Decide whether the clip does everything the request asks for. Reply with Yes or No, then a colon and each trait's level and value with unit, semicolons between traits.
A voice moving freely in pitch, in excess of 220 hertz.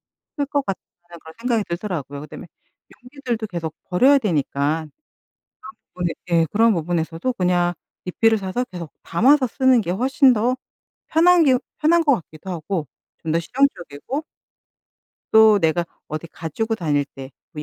No: wide, 7.3 semitones; medium, 185 Hz